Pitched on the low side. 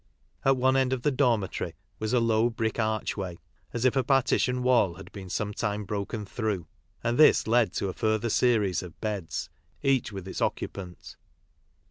Yes: low, 110 Hz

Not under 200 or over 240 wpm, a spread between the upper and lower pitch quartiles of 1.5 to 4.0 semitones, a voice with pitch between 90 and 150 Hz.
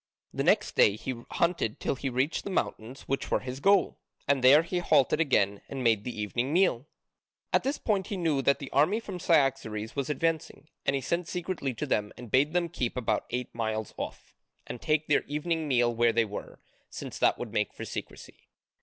No: fast, 205 wpm; wide, 5.6 semitones; low, 135 Hz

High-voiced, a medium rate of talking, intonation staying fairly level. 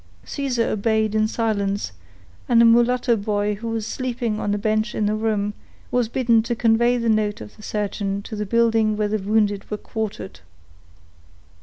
Yes: high, 220 Hz; average, 175 wpm; narrow, 1.9 semitones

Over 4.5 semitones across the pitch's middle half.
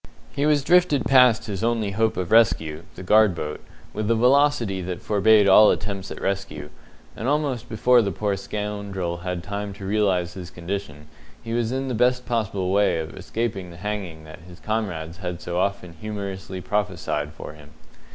No: average, 4.0 semitones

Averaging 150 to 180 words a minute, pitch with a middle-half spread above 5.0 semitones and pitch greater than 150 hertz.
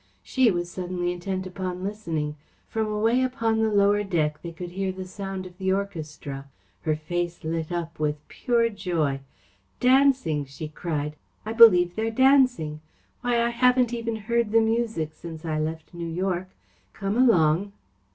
Yes: average, 160 wpm; wide, 5.6 semitones; medium, 185 Hz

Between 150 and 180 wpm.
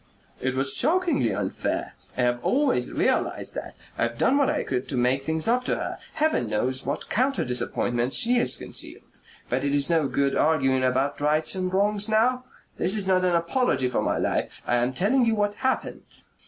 No: average, 195 wpm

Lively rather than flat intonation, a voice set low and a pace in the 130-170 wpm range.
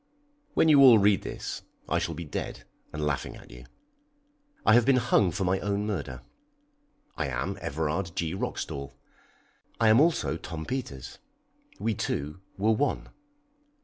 Yes: wide, 6.5 semitones; very low, 95 Hz; average, 150 wpm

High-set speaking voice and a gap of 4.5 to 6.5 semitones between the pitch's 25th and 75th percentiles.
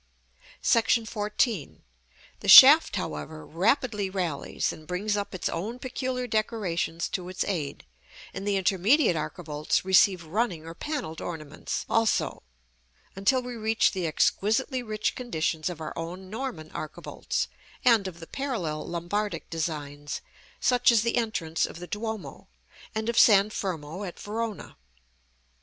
Yes: high, 195 Hz; wide, 5.4 semitones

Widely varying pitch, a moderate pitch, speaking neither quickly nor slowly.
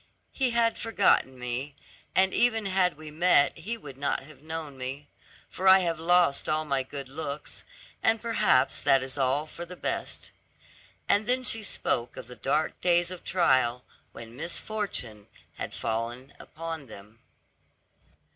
Yes: wide, 5.7 semitones; medium, 155 Hz; average, 155 wpm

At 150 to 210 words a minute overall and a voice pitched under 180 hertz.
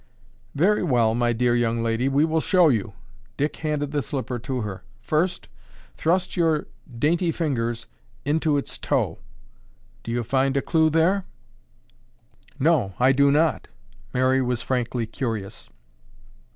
No: average, 140 wpm; low, 135 Hz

